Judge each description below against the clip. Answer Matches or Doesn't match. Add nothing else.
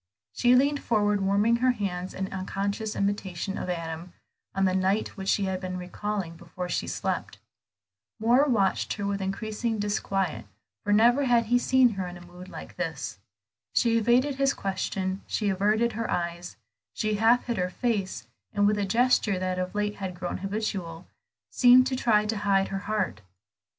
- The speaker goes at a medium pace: Matches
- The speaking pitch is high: Matches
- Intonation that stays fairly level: Doesn't match